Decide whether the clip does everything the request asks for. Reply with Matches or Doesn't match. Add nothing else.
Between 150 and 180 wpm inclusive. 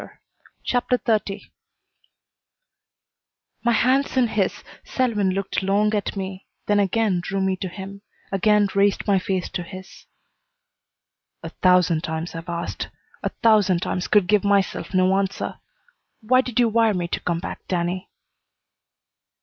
Doesn't match